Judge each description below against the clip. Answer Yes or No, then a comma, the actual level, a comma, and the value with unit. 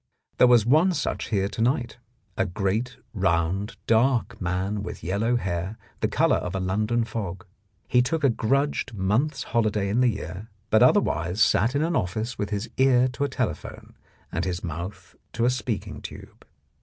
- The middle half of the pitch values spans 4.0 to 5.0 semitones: Yes, average, 4.4 semitones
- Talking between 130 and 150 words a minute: No, average, 180 wpm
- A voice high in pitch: No, low, 110 Hz